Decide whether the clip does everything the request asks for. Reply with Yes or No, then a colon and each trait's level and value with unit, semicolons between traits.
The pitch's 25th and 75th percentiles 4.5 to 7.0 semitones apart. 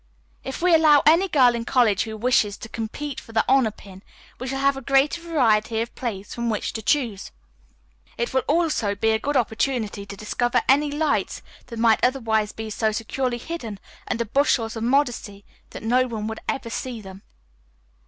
No: average, 3.7 semitones